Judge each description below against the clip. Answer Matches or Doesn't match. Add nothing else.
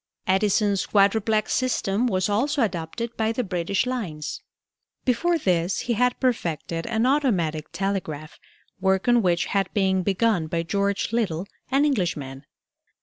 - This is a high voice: Matches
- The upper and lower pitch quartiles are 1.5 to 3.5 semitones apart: Doesn't match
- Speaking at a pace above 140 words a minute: Doesn't match